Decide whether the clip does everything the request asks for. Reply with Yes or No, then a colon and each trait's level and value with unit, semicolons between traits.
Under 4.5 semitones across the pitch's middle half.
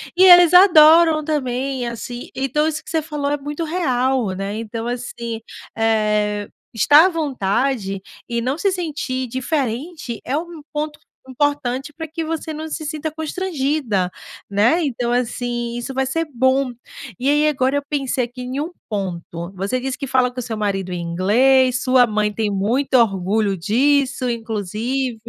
No: average, 4.8 semitones